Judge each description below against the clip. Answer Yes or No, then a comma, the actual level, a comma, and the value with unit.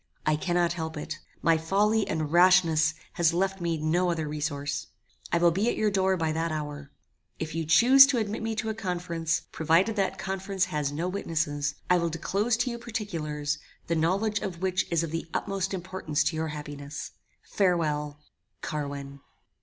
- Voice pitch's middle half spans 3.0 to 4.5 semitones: Yes, average, 3.8 semitones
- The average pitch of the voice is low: No, medium, 170 Hz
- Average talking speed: Yes, average, 175 wpm